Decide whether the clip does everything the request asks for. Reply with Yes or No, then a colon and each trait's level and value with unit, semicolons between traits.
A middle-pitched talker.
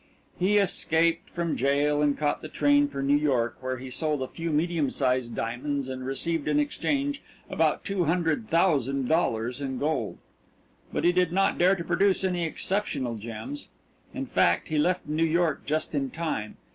Yes: medium, 150 Hz